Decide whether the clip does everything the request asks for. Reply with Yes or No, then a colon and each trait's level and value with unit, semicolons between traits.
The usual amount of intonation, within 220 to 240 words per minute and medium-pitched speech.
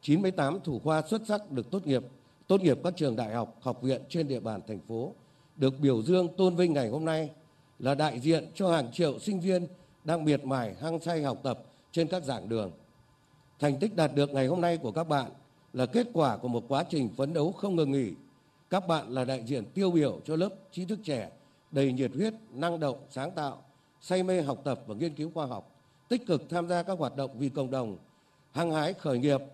Yes: average, 4.1 semitones; average, 230 wpm; medium, 145 Hz